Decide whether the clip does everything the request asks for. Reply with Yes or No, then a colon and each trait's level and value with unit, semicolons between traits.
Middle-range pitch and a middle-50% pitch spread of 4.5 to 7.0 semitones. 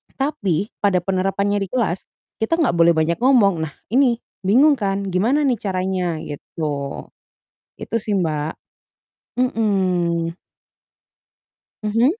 No: high, 195 Hz; average, 5.1 semitones